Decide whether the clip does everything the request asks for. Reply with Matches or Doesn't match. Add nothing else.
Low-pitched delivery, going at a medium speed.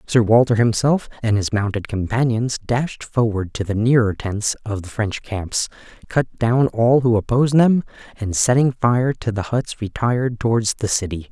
Matches